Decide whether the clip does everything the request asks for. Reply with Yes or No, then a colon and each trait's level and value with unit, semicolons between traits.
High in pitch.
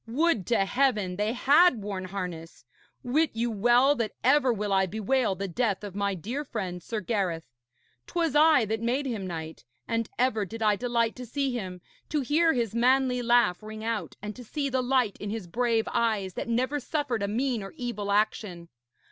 Yes: high, 230 Hz